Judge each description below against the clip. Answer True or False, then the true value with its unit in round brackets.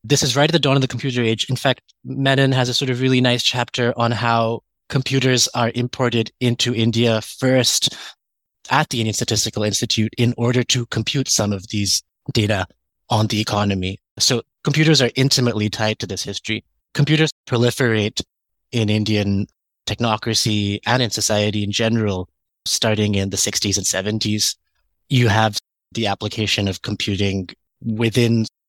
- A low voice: True (115 Hz)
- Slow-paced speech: False (155 wpm)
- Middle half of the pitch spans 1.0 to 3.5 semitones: True (2.9 semitones)